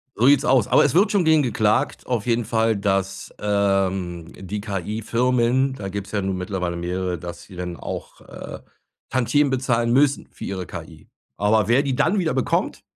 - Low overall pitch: Yes, low, 110 Hz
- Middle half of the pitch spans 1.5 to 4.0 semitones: No, average, 5.0 semitones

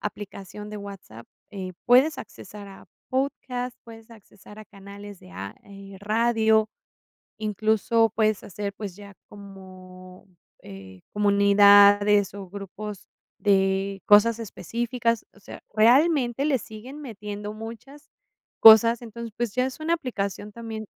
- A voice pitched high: Yes, high, 210 Hz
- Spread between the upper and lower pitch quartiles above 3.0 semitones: No, narrow, 2.6 semitones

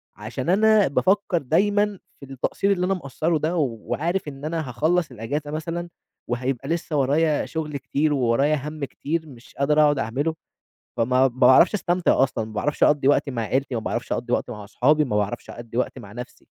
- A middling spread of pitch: Yes, average, 4.7 semitones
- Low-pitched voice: No, medium, 145 Hz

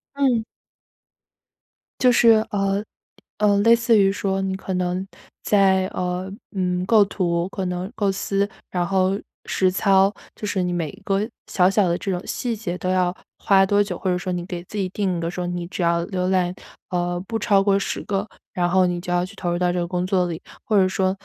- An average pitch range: No, narrow, 1.8 semitones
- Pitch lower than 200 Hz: Yes, high, 190 Hz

